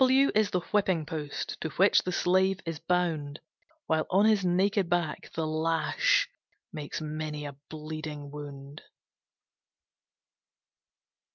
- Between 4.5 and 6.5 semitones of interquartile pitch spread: No, average, 3.7 semitones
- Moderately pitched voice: Yes, medium, 160 Hz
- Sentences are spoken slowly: Yes, slow, 125 wpm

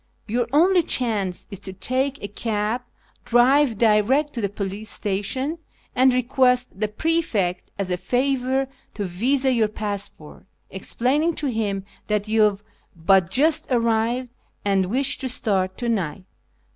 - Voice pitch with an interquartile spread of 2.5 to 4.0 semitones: No, average, 4.6 semitones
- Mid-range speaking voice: No, high, 225 Hz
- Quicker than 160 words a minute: No, average, 145 wpm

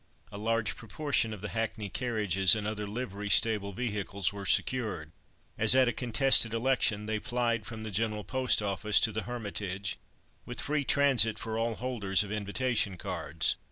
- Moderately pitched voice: No, low, 110 Hz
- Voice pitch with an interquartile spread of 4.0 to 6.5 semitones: No, average, 2.8 semitones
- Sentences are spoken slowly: No, average, 165 wpm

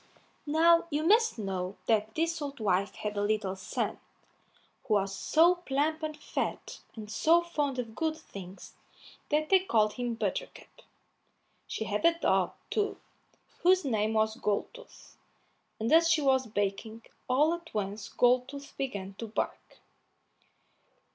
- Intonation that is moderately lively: No, wide, 7.2 semitones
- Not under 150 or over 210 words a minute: No, average, 140 wpm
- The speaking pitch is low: No, very high, 255 Hz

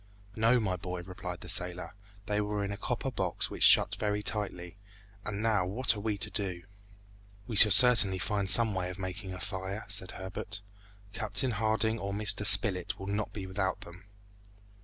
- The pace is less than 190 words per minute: Yes, average, 180 wpm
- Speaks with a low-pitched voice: Yes, low, 100 Hz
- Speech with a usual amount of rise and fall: No, narrow, 2.2 semitones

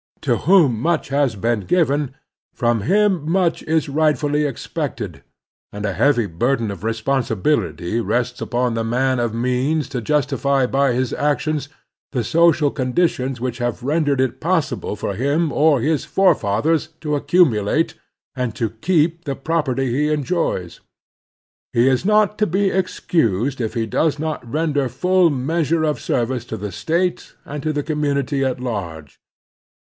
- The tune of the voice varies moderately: Yes, average, 4.8 semitones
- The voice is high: No, medium, 140 Hz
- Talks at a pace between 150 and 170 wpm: Yes, average, 155 wpm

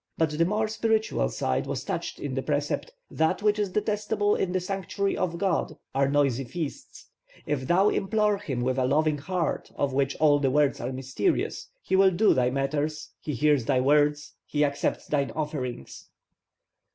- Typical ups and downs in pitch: No, wide, 5.8 semitones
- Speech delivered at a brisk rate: No, average, 175 wpm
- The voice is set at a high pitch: No, medium, 150 Hz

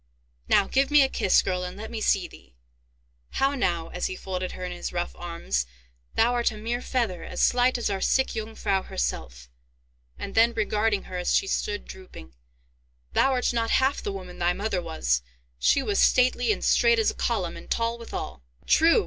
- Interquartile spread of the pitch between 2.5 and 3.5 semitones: No, wide, 5.5 semitones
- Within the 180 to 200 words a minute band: Yes, average, 190 wpm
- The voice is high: Yes, high, 205 Hz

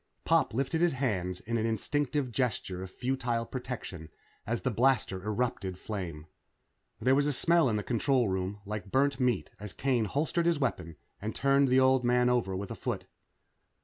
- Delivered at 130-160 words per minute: No, average, 180 wpm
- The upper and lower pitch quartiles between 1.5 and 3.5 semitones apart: No, average, 4.9 semitones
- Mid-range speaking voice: No, low, 120 Hz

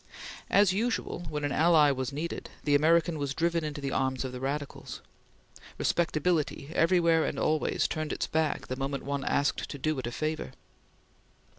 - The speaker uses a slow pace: No, average, 170 wpm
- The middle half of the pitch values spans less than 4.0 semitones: Yes, average, 3.1 semitones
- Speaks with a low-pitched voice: No, medium, 150 Hz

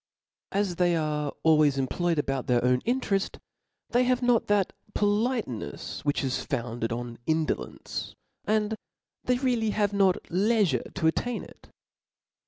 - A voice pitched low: No, medium, 180 Hz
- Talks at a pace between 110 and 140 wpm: Yes, slow, 135 wpm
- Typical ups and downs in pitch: No, wide, 7.6 semitones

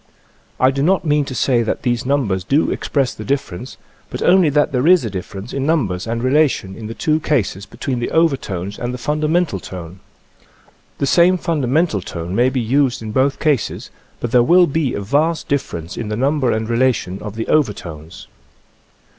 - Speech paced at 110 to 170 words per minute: No, average, 195 wpm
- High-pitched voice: No, low, 125 Hz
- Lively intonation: Yes, wide, 5.8 semitones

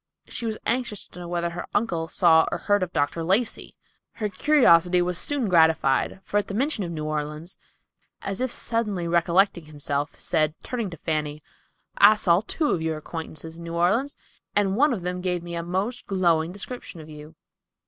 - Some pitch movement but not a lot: Yes, average, 4.2 semitones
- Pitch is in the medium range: Yes, medium, 175 Hz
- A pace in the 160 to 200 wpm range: Yes, average, 190 wpm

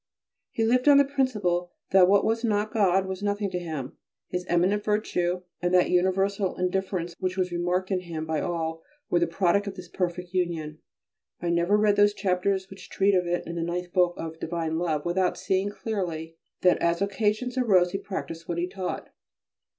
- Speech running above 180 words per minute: Yes, average, 190 wpm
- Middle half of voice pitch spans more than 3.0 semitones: No, narrow, 2.6 semitones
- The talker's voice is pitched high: No, medium, 180 Hz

